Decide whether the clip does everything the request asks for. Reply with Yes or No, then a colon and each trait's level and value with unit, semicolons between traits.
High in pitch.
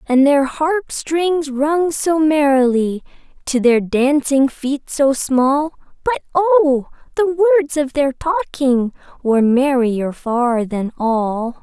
Yes: very high, 280 Hz